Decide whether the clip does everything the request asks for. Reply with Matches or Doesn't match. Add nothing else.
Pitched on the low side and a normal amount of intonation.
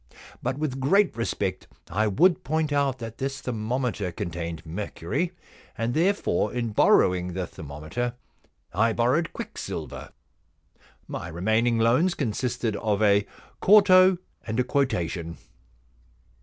Doesn't match